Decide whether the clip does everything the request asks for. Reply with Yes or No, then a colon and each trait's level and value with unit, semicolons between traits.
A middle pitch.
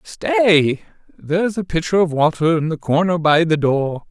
Yes: medium, 165 Hz